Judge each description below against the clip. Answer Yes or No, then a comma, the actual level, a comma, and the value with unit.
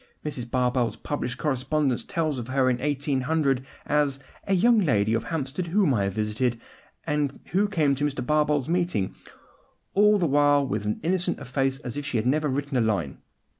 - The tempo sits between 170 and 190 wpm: Yes, average, 180 wpm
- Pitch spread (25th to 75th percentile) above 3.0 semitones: Yes, average, 3.6 semitones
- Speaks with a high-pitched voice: No, medium, 140 Hz